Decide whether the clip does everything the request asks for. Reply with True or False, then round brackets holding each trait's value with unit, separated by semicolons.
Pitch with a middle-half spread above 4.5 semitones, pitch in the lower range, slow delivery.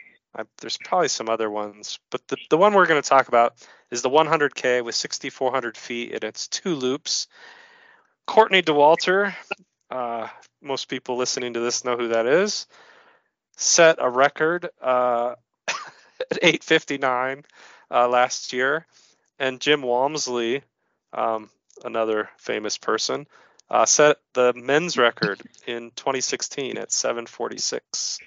True (5.3 semitones; 130 Hz; 130 wpm)